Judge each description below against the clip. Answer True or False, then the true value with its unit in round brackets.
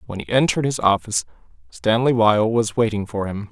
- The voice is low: True (110 Hz)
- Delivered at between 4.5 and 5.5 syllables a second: False (5.8 syllables/s)